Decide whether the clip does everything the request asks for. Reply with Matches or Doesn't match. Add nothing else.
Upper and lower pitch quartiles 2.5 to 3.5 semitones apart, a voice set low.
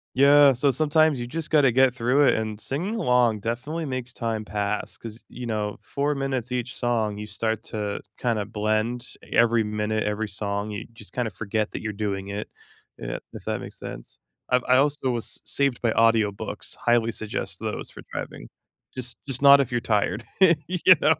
Doesn't match